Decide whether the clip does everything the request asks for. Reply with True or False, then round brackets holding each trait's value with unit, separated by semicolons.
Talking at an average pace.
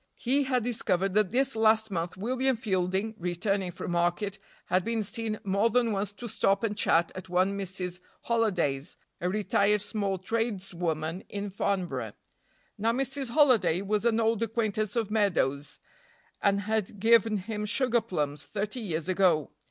True (150 wpm)